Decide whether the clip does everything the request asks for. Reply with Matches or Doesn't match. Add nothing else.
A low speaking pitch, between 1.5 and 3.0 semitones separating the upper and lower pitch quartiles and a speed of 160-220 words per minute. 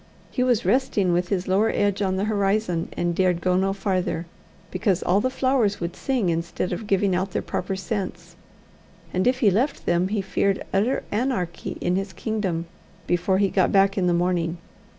Doesn't match